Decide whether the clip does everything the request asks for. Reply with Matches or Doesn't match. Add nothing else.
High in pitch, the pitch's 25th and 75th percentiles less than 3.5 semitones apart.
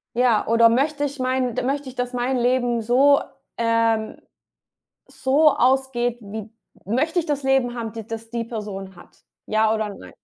Matches